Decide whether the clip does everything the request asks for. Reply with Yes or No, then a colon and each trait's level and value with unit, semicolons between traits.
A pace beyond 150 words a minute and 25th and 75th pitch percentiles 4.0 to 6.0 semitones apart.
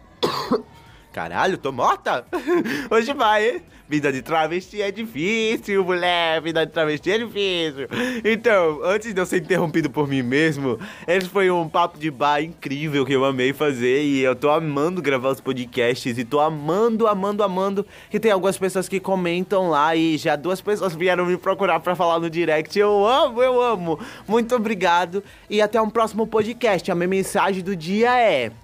Yes: average, 175 wpm; average, 5.1 semitones